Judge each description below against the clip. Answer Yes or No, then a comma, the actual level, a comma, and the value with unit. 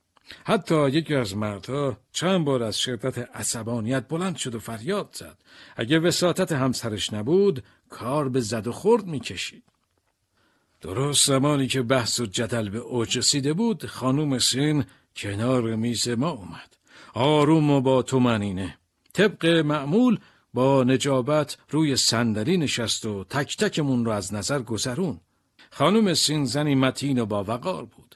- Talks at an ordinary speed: Yes, average, 140 wpm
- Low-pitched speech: Yes, low, 130 Hz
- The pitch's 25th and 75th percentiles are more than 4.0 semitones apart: Yes, average, 4.4 semitones